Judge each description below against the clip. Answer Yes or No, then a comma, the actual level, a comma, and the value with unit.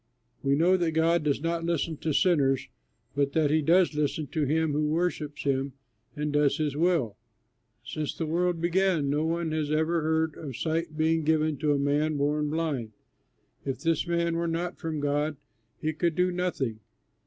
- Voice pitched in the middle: Yes, medium, 155 Hz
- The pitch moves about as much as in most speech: No, narrow, 2.3 semitones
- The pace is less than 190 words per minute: Yes, average, 180 wpm